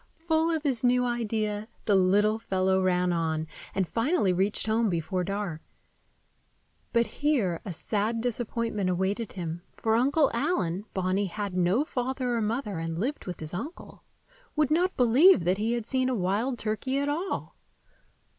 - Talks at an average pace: Yes, average, 155 wpm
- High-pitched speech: Yes, high, 220 Hz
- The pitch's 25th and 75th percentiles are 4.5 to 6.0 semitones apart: Yes, wide, 5.5 semitones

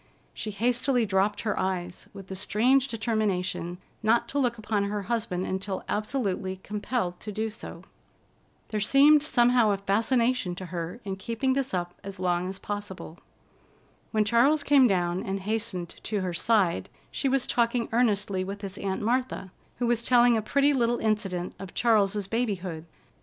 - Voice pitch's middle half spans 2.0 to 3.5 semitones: No, average, 3.9 semitones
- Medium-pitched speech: No, high, 210 Hz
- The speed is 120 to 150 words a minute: No, average, 165 wpm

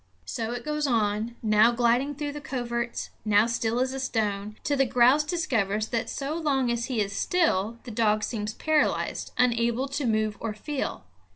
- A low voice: No, high, 235 Hz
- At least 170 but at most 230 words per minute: Yes, average, 180 wpm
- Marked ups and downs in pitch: No, average, 3.9 semitones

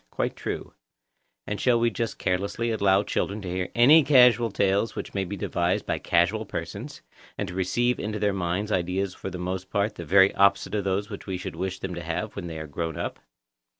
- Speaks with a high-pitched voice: No, low, 100 Hz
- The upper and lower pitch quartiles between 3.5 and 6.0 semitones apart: No, average, 2.8 semitones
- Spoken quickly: Yes, fast, 215 wpm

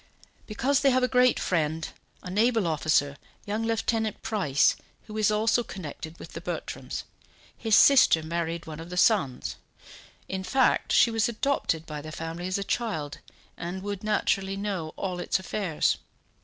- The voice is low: No, high, 190 Hz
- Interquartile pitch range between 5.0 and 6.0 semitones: Yes, wide, 5.5 semitones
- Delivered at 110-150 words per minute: No, average, 160 wpm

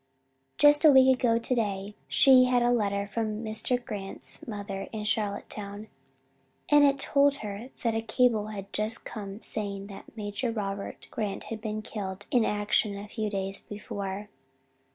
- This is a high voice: Yes, high, 215 Hz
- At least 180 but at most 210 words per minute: No, average, 155 wpm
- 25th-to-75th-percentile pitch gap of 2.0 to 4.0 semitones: Yes, average, 2.8 semitones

